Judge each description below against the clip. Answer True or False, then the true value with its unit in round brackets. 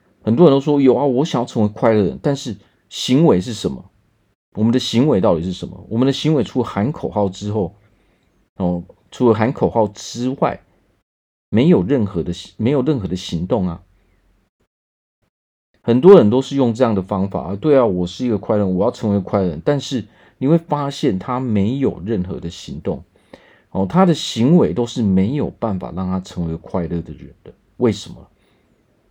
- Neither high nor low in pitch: False (105 Hz)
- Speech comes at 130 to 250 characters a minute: False (270 characters per minute)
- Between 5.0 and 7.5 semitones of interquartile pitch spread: True (5.3 semitones)